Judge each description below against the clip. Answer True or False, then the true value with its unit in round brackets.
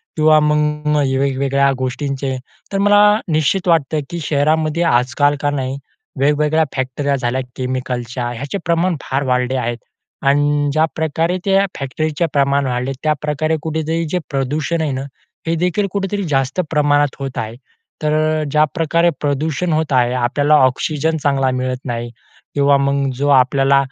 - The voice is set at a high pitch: False (145 Hz)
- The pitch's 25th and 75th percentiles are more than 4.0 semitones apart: False (3.0 semitones)